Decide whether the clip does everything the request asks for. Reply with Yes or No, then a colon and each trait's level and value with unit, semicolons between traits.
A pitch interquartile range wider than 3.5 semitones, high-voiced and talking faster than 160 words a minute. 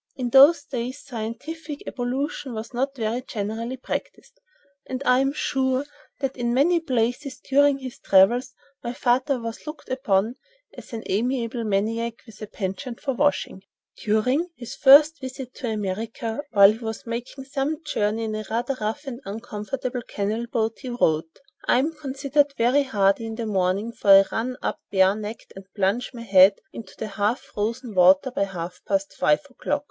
Yes: average, 3.9 semitones; high, 235 Hz; average, 170 wpm